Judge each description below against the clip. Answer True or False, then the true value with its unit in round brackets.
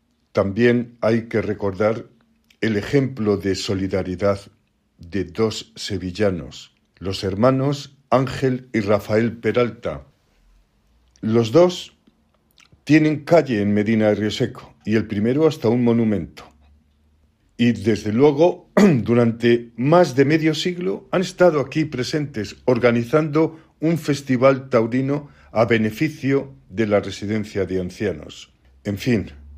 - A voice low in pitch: True (115 Hz)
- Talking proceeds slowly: True (115 wpm)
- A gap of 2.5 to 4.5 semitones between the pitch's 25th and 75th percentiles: False (5.1 semitones)